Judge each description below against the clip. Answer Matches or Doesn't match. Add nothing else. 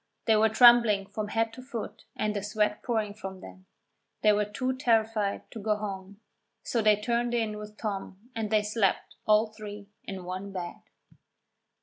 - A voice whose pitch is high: Matches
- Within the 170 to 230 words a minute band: Matches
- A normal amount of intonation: Doesn't match